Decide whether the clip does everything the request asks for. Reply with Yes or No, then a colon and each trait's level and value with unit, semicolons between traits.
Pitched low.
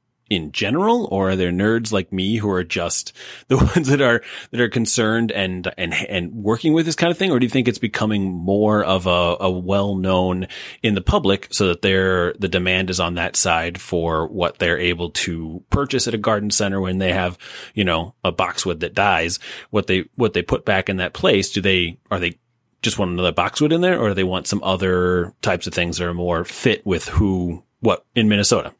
Yes: very low, 95 Hz